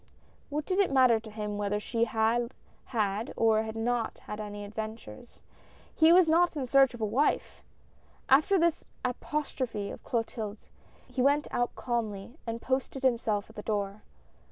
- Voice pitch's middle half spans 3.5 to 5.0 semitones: Yes, average, 4.0 semitones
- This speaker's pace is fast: No, average, 160 wpm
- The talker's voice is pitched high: Yes, high, 230 Hz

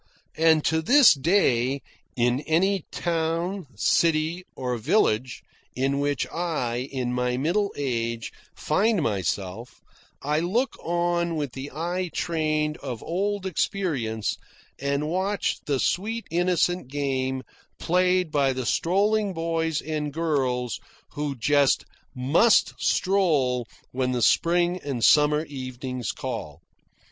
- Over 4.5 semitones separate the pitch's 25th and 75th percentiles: Yes, average, 5.2 semitones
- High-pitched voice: No, medium, 150 Hz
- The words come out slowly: Yes, slow, 115 wpm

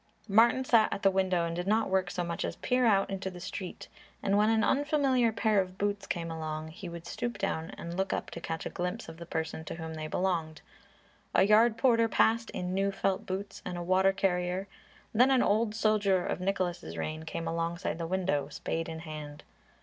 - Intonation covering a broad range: No, average, 4.0 semitones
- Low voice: No, medium, 185 Hz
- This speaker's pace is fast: Yes, fast, 210 wpm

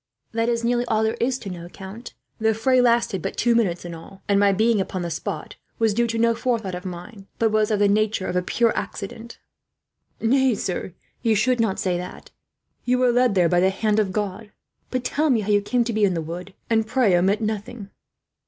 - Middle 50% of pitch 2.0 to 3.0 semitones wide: No, average, 3.5 semitones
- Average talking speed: No, fast, 225 wpm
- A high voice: Yes, high, 215 Hz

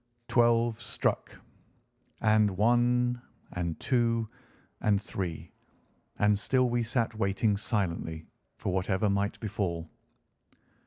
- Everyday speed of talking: No, slow, 100 wpm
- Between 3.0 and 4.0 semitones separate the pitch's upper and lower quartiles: Yes, average, 3.5 semitones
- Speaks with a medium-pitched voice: No, low, 105 Hz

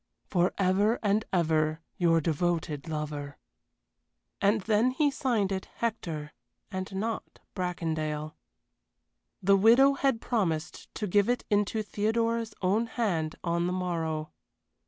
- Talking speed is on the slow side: Yes, slow, 120 wpm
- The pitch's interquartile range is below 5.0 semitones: No, average, 5.3 semitones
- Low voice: No, high, 190 Hz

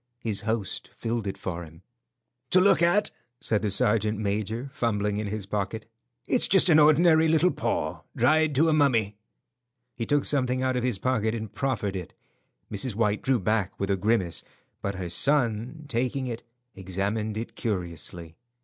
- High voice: No, low, 110 Hz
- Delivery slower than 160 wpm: No, average, 165 wpm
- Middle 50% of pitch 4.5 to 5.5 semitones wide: Yes, average, 4.9 semitones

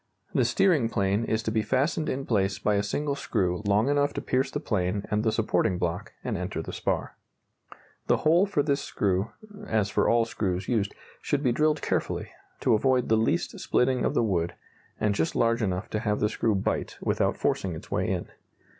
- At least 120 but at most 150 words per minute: No, average, 200 wpm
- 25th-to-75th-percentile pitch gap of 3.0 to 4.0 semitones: No, average, 4.8 semitones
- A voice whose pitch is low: Yes, low, 110 Hz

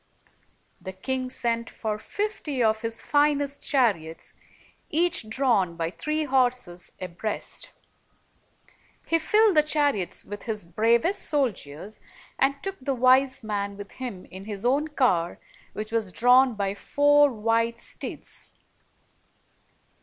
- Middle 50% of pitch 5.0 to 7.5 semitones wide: Yes, wide, 5.5 semitones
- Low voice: No, high, 235 Hz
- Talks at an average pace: No, slow, 125 wpm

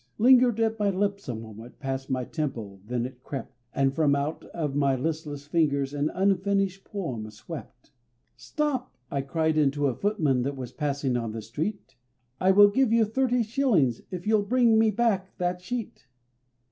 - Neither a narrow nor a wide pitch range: No, wide, 7.3 semitones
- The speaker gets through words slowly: No, average, 170 wpm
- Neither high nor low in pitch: Yes, medium, 160 Hz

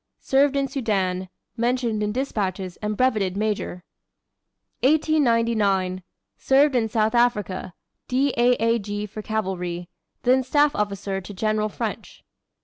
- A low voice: No, high, 215 Hz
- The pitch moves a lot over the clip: No, average, 4.4 semitones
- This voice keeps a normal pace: No, slow, 125 wpm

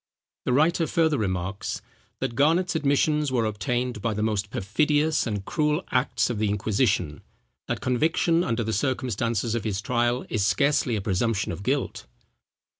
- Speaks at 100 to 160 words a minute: Yes, average, 150 wpm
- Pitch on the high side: No, low, 120 Hz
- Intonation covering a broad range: Yes, wide, 5.7 semitones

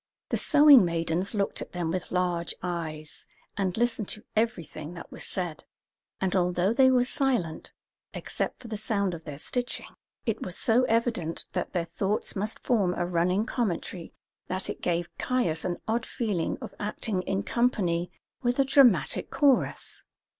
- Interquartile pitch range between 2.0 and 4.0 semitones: No, average, 5.3 semitones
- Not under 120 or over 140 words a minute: No, average, 160 wpm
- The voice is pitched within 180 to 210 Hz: Yes, high, 190 Hz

